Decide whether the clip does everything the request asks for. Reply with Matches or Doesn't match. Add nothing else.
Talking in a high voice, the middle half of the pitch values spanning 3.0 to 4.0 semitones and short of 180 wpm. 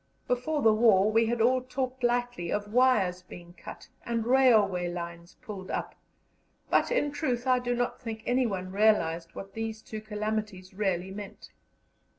Doesn't match